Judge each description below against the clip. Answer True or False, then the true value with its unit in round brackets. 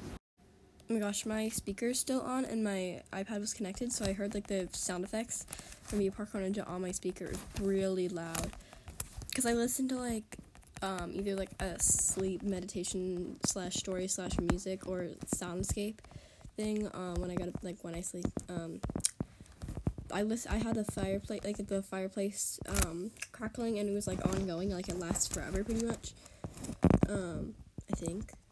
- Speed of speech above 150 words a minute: True (170 wpm)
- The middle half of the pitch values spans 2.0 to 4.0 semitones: True (2.8 semitones)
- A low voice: False (195 Hz)